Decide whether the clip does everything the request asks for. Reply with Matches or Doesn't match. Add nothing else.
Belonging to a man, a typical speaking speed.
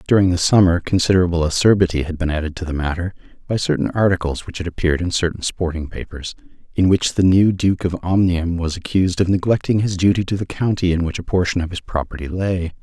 Doesn't match